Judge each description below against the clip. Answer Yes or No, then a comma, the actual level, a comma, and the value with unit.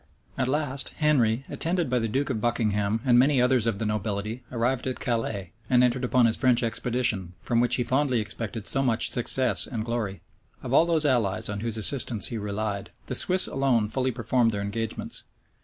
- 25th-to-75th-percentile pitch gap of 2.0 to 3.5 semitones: Yes, average, 3.1 semitones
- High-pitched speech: No, low, 120 Hz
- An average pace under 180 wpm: No, average, 190 wpm